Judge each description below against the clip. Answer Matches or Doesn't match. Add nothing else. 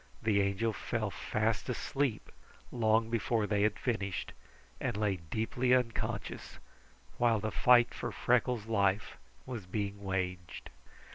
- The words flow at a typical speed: Doesn't match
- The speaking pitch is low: Matches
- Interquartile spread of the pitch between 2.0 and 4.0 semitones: Matches